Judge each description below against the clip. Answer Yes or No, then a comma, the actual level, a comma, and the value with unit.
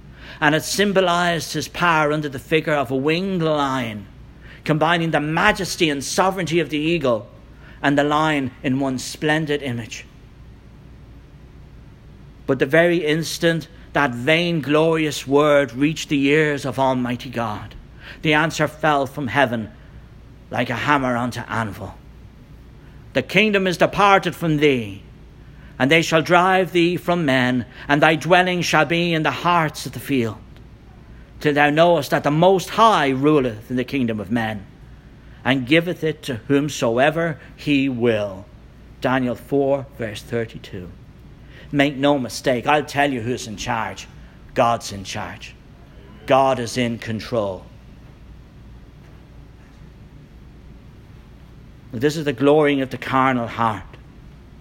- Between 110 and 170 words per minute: Yes, slow, 135 wpm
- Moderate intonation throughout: Yes, average, 4.2 semitones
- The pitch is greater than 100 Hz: Yes, medium, 140 Hz